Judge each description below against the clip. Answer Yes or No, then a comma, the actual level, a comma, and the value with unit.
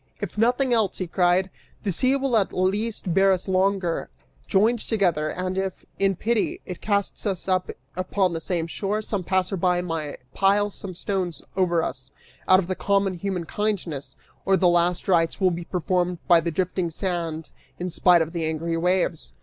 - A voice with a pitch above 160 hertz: Yes, medium, 185 Hz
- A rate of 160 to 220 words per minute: Yes, average, 175 wpm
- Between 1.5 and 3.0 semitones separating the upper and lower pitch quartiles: Yes, narrow, 2.4 semitones